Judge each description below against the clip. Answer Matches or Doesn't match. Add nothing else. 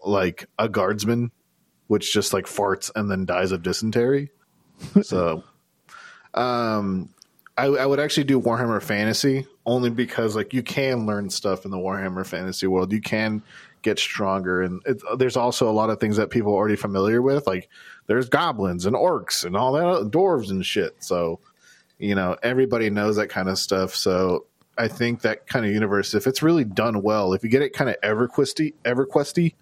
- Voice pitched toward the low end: Matches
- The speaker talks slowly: Doesn't match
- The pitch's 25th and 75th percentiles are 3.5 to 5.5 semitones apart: Matches